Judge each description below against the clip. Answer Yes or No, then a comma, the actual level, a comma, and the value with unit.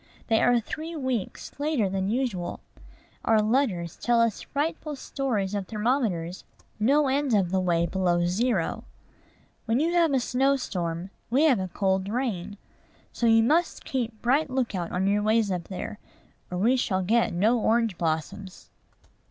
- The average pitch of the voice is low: No, high, 220 Hz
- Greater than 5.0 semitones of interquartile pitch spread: Yes, wide, 5.5 semitones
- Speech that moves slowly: No, average, 160 wpm